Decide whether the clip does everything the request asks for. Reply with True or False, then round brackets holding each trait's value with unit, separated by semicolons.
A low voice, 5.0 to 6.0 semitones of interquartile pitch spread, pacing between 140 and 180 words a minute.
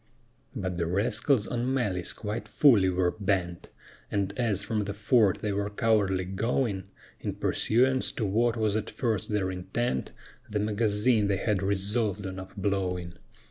False (105 Hz; 2.9 semitones; 155 wpm)